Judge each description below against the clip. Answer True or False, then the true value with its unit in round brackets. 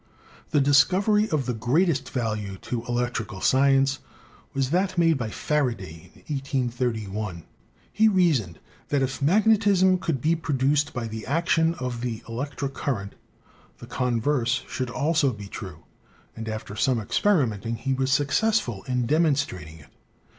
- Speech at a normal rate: True (145 wpm)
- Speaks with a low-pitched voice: True (130 Hz)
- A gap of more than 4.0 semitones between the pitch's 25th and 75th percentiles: True (5.1 semitones)